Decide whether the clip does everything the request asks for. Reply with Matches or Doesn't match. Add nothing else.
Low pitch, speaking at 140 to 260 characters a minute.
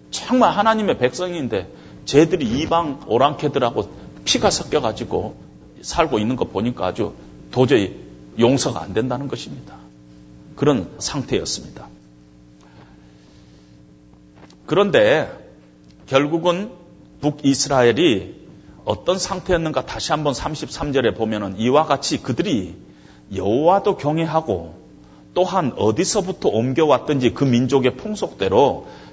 Matches